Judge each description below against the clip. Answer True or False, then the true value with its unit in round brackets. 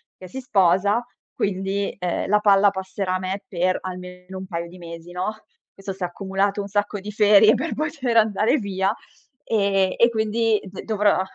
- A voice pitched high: True (195 Hz)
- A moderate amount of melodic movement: False (2.2 semitones)